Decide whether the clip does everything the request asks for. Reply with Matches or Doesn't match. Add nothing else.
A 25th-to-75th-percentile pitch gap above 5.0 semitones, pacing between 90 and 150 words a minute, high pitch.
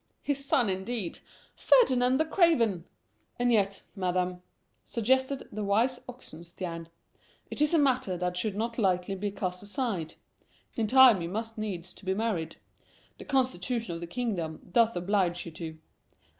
Matches